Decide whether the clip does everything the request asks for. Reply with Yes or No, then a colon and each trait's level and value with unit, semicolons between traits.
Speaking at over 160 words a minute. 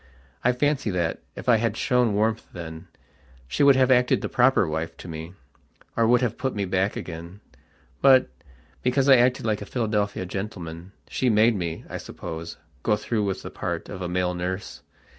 Yes: average, 185 wpm